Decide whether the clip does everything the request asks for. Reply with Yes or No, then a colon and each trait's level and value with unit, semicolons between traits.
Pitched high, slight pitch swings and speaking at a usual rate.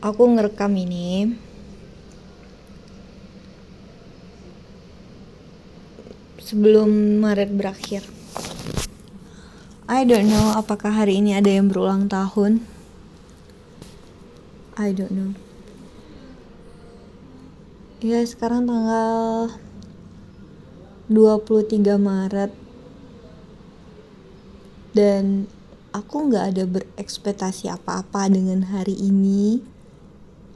No: high, 205 Hz; narrow, 1.8 semitones; slow, 65 wpm